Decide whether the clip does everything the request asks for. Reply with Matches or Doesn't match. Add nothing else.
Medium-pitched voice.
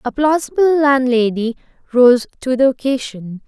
Doesn't match